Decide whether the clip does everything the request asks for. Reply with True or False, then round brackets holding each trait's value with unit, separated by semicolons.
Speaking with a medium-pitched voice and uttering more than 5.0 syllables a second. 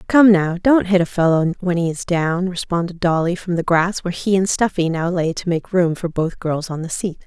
True (175 Hz; 5.2 syllables/s)